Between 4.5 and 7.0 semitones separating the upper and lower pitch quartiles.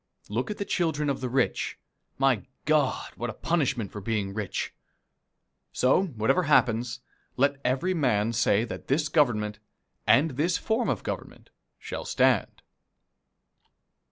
Yes: average, 5.2 semitones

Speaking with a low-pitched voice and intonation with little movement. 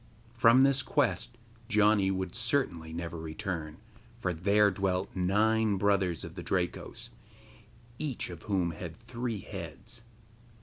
No: low, 100 Hz; average, 4.5 semitones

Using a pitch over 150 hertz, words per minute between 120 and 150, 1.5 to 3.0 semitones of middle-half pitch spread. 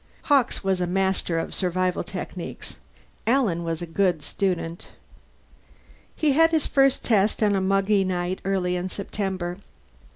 Yes: high, 190 Hz; average, 140 wpm; average, 2.7 semitones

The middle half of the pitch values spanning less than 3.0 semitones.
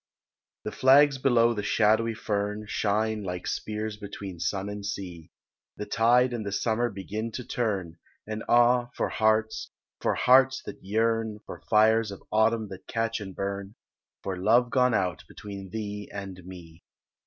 Yes: narrow, 2.5 semitones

